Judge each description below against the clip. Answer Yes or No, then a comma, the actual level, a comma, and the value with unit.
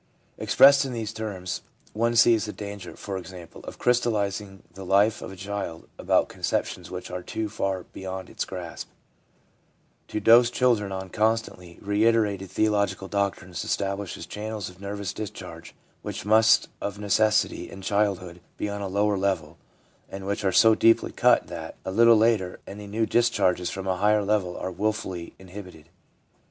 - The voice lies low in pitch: Yes, low, 100 Hz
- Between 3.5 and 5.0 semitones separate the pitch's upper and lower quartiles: No, narrow, 2.5 semitones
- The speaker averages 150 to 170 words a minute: Yes, average, 160 wpm